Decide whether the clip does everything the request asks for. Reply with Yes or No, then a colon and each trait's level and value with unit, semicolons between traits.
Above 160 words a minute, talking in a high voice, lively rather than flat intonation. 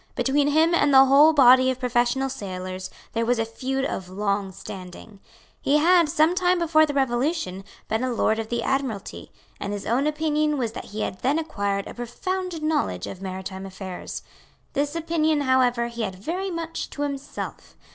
Yes: average, 180 wpm; very high, 260 Hz; wide, 6.8 semitones